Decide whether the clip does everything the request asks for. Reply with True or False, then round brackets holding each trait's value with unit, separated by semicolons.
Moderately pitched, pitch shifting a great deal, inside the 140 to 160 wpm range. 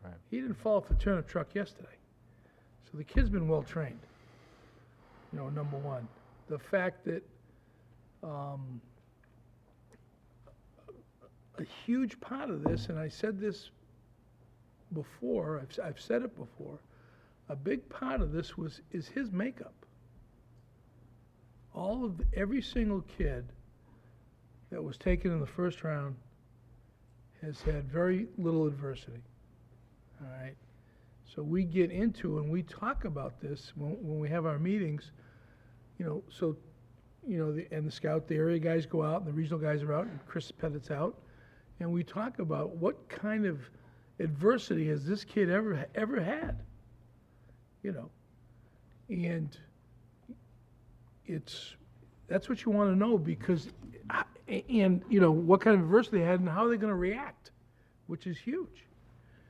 True (150 Hz; 7.0 semitones; 150 wpm)